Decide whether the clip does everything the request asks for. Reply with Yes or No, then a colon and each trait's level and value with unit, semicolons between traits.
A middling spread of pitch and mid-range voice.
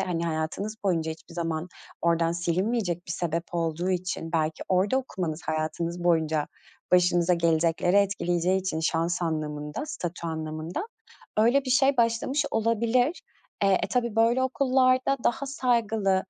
No: wide, 5.7 semitones; medium, 180 Hz